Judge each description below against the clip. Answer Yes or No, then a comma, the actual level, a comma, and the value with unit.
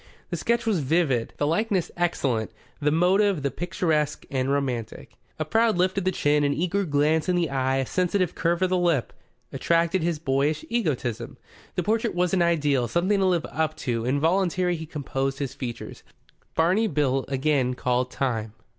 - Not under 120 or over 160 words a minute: No, average, 175 wpm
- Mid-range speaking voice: Yes, medium, 160 Hz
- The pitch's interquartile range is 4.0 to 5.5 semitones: Yes, average, 4.9 semitones